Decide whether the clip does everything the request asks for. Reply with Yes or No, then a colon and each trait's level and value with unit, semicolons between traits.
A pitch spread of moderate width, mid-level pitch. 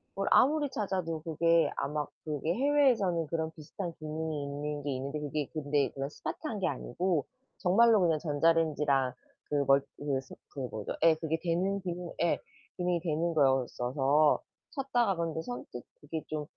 Yes: average, 3.5 semitones; medium, 160 Hz